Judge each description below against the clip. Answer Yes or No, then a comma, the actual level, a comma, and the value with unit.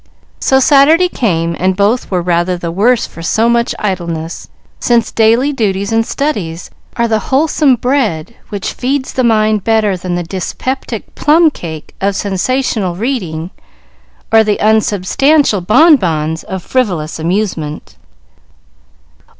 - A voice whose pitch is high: Yes, high, 215 Hz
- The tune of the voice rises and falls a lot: Yes, wide, 6.1 semitones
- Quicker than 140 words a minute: No, slow, 135 wpm